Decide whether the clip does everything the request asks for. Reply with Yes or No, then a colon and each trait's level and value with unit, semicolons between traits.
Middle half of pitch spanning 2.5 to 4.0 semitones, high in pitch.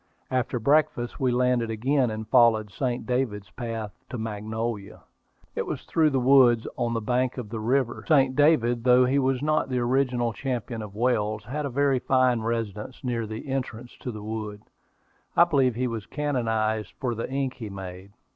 No: average, 3.0 semitones; low, 120 Hz